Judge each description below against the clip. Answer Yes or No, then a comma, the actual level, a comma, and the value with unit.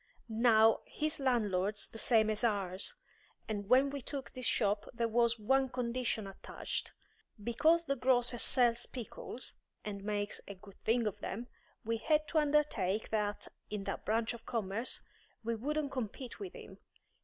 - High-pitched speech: Yes, high, 230 Hz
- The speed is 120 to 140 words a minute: No, average, 155 wpm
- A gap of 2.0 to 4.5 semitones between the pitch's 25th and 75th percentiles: Yes, average, 3.6 semitones